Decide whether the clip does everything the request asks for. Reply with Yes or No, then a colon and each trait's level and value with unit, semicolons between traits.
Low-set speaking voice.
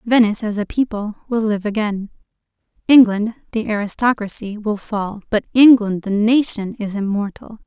No: high, 215 Hz